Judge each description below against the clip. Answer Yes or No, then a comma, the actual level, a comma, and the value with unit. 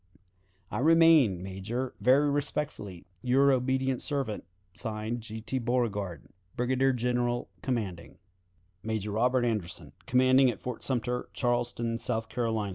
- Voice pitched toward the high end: No, low, 120 Hz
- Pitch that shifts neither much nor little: Yes, average, 3.0 semitones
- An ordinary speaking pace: No, slow, 120 wpm